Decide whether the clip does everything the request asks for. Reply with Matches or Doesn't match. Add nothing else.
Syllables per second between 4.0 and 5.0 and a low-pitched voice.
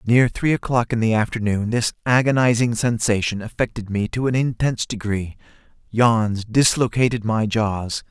Matches